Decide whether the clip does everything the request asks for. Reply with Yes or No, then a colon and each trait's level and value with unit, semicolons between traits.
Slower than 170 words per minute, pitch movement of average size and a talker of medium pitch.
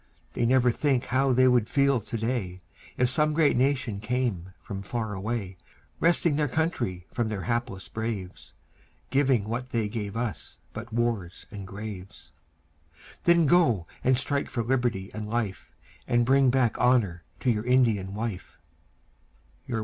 No: average, 150 wpm; average, 4.0 semitones; low, 120 Hz